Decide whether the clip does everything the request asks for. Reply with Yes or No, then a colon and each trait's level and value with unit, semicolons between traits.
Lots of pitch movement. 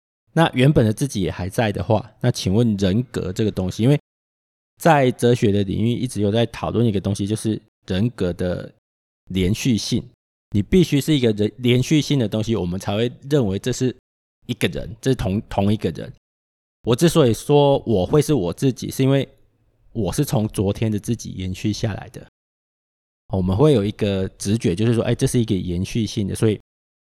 No: average, 4.3 semitones